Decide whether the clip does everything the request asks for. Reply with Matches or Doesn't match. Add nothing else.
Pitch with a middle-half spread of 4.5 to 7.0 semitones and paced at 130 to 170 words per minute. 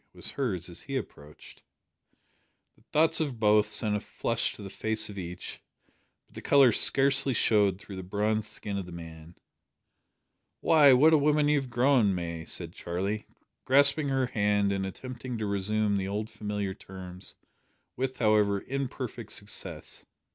Matches